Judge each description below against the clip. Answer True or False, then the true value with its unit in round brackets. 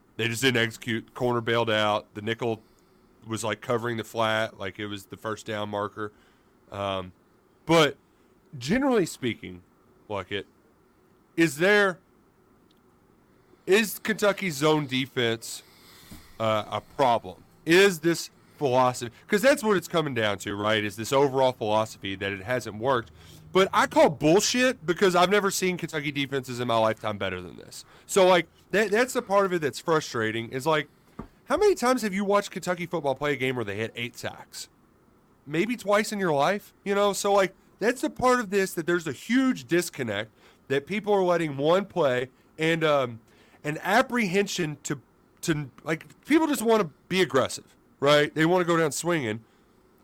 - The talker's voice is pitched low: False (150 Hz)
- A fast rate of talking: False (175 wpm)